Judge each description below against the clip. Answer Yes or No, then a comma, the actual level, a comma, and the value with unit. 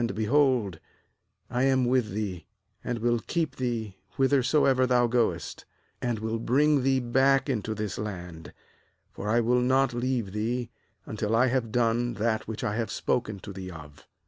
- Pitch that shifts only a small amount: No, average, 3.3 semitones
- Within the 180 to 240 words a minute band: No, average, 165 wpm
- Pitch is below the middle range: Yes, low, 120 Hz